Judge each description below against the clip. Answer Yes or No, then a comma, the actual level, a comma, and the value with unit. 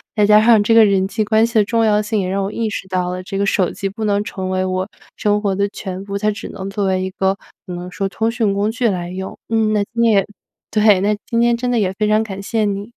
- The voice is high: Yes, high, 205 Hz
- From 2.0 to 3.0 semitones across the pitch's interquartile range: Yes, narrow, 2.4 semitones